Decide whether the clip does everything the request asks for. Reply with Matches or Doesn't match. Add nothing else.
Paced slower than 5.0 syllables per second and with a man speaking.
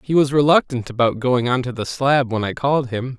Doesn't match